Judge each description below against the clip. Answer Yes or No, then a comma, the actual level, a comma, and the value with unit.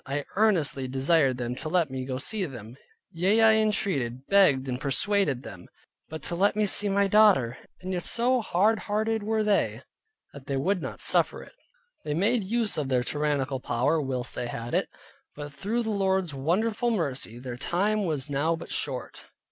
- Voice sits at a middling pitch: Yes, medium, 165 Hz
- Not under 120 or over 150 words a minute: No, average, 190 wpm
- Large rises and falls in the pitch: Yes, wide, 7.5 semitones